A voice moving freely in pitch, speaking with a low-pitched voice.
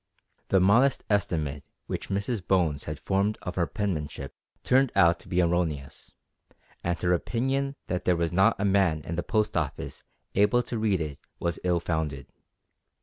No: average, 4.0 semitones; very low, 90 Hz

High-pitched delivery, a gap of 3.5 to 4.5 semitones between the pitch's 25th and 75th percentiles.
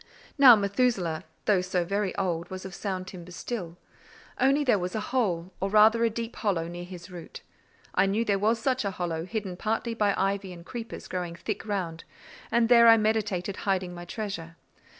Yes: high, 195 Hz; average, 3.9 semitones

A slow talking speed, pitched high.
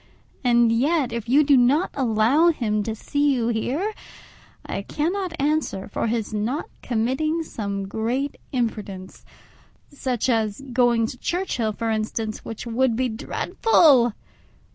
Yes: slow, 130 wpm; high, 240 Hz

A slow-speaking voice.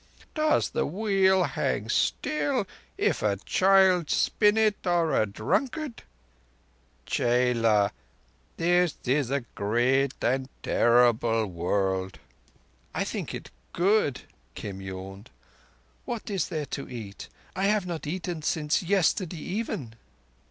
Yes: slow, 115 wpm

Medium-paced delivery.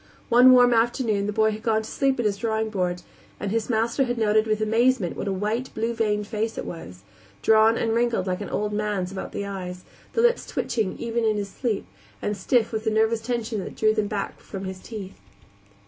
No: fast, 220 wpm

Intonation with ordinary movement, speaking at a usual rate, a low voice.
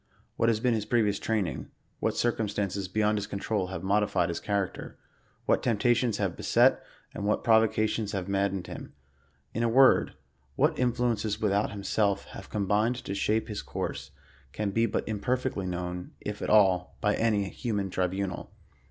No: narrow, 2.3 semitones; average, 175 wpm; low, 105 Hz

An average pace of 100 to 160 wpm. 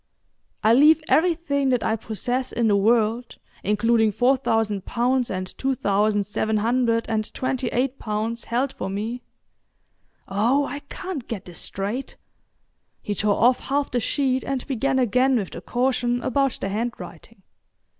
Yes: average, 150 wpm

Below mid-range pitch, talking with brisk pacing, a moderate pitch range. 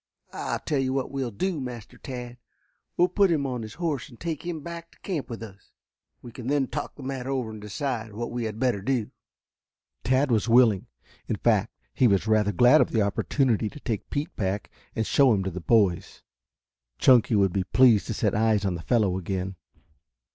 Yes: low, 120 Hz; fast, 210 wpm; average, 4.4 semitones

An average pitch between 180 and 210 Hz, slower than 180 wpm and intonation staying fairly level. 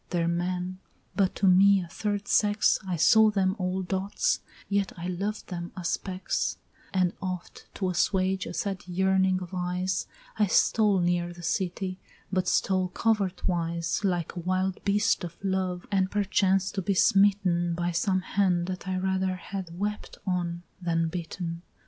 Yes: medium, 185 Hz; average, 160 wpm; narrow, 1.8 semitones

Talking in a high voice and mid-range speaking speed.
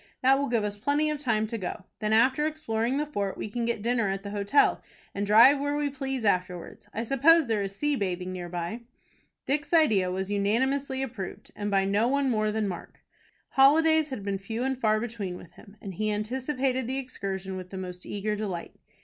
No: high, 220 Hz; fast, 210 wpm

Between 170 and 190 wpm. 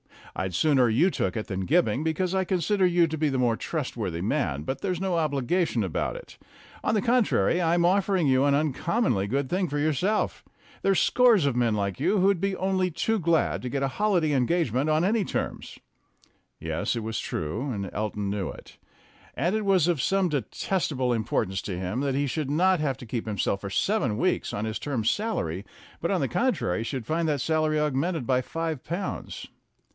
No: average, 200 wpm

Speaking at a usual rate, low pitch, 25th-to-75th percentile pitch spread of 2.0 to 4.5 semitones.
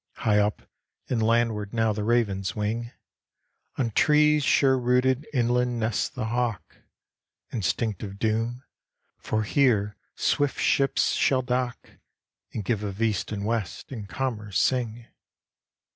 No: slow, 130 wpm; low, 115 Hz; average, 2.9 semitones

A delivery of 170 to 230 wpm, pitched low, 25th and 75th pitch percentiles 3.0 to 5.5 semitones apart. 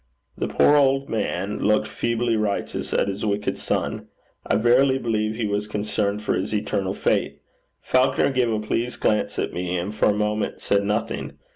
No: average, 175 wpm; low, 105 Hz; narrow, 2.5 semitones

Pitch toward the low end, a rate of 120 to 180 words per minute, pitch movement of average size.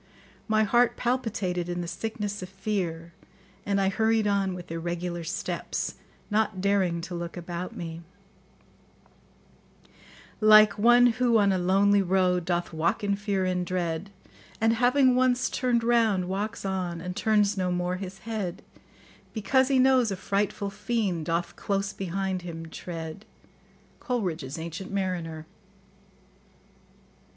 No: high, 195 Hz; slow, 135 wpm; average, 3.6 semitones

